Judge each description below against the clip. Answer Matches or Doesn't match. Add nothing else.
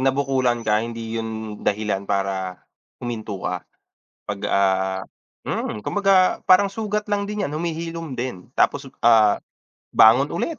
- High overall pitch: Doesn't match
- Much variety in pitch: Matches